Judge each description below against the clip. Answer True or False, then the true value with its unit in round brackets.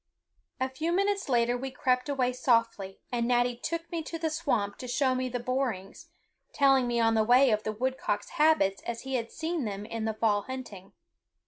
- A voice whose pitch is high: True (250 Hz)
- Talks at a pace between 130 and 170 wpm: False (200 wpm)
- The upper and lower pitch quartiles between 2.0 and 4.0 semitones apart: True (3.4 semitones)